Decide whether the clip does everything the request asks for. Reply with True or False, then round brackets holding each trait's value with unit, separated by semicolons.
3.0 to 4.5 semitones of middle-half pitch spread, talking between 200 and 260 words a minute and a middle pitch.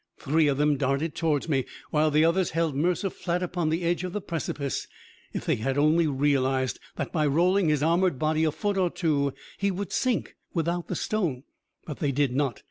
True (3.5 semitones; 205 wpm; 155 Hz)